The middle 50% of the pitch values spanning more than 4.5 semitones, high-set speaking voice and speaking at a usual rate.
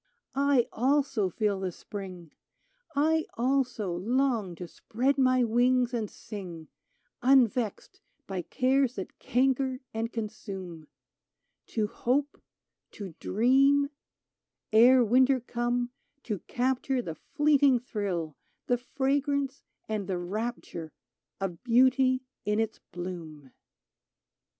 No: average, 5.0 semitones; high, 240 Hz; slow, 110 wpm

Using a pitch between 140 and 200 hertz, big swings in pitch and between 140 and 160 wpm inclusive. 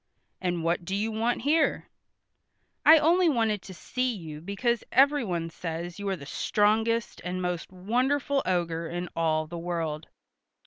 Yes: high, 190 Hz; wide, 5.9 semitones; average, 150 wpm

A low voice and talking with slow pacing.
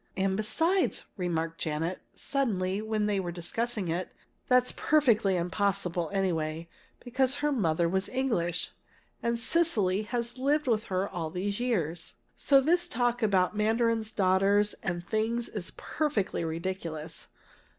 No: high, 205 Hz; slow, 130 wpm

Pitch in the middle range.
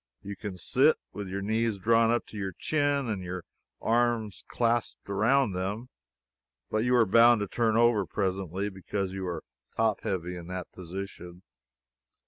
No: low, 105 Hz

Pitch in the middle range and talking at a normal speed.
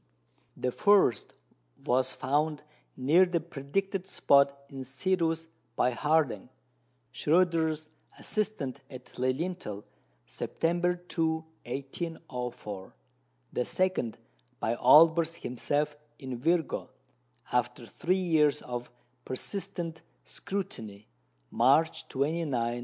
No: medium, 150 Hz; slow, 90 wpm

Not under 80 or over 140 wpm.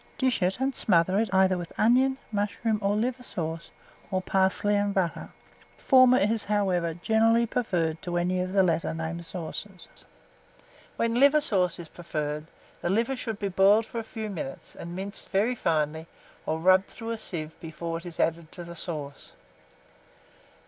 No: average, 170 wpm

